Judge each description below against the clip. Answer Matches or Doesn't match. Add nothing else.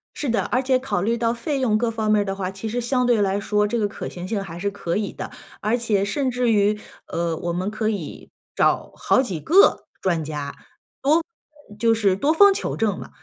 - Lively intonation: Doesn't match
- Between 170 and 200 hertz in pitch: Doesn't match